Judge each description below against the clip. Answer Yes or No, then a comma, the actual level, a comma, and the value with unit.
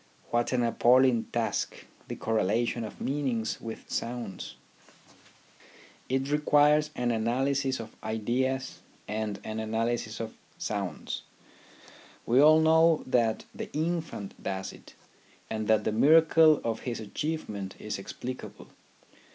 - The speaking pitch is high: No, low, 120 Hz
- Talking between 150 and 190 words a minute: No, average, 140 wpm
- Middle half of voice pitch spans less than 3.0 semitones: No, average, 4.1 semitones